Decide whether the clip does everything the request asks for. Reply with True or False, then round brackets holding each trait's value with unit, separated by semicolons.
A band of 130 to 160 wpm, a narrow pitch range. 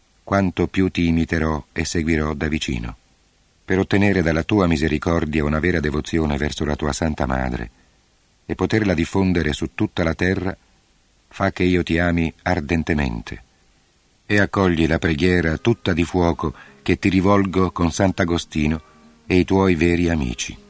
False (150 wpm; 3.2 semitones)